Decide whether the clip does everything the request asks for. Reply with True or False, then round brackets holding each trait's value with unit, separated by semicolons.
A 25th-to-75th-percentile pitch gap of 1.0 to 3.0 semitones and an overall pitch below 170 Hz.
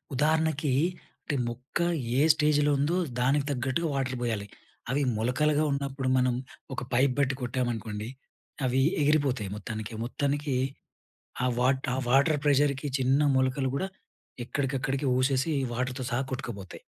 True (2.5 semitones; 135 Hz)